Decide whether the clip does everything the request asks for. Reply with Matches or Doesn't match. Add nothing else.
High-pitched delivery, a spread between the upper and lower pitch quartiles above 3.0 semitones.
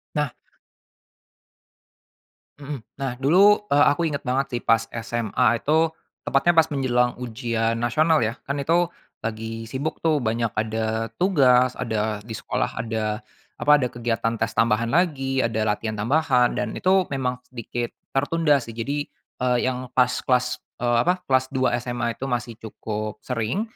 Doesn't match